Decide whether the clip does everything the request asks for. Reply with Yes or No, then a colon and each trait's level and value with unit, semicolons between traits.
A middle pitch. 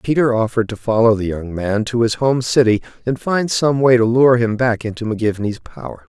No: low, 115 Hz